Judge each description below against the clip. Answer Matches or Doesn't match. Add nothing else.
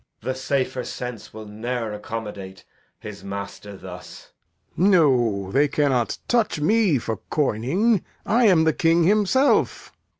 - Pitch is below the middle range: Matches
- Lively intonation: Matches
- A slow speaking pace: Matches